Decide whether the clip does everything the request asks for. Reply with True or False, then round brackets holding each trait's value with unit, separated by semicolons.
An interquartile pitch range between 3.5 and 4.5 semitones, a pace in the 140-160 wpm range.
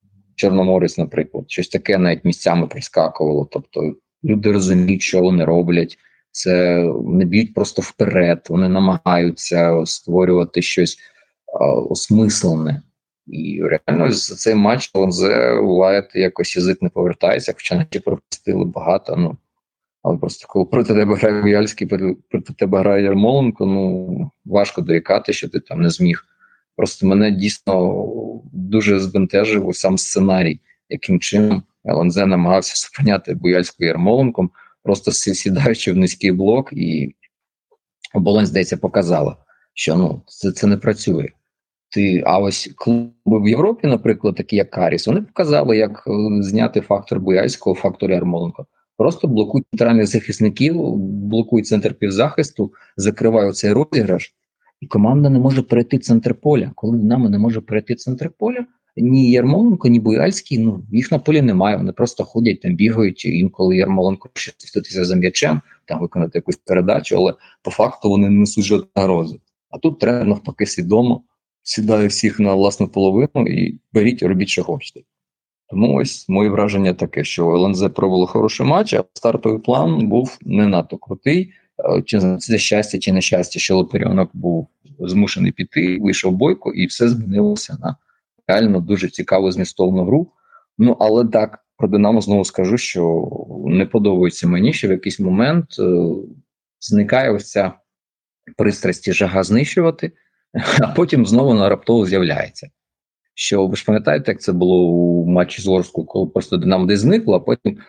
True (3.8 semitones; 145 wpm)